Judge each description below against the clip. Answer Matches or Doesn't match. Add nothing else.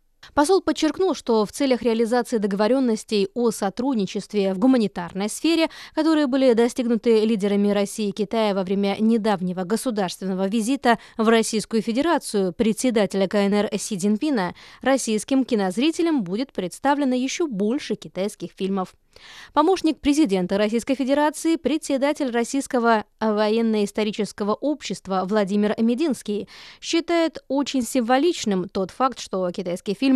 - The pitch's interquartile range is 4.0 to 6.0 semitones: Matches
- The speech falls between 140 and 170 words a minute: Doesn't match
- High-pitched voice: Matches